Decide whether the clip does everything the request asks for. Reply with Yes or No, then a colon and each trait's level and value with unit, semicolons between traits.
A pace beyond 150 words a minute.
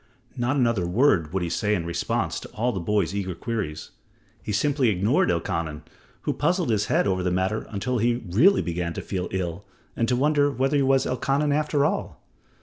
Yes: average, 195 wpm